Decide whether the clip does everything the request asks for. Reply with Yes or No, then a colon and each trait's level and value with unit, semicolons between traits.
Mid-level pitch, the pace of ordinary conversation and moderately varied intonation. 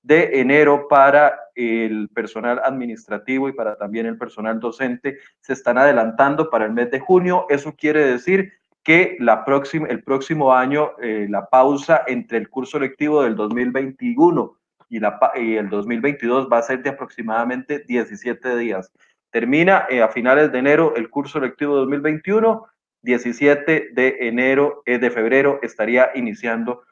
No: low, 130 Hz; average, 150 wpm; average, 3.7 semitones